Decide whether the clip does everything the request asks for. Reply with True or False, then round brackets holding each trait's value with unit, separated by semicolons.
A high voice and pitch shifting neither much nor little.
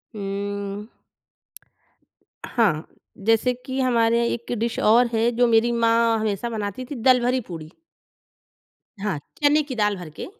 True (230 Hz; 3.0 semitones)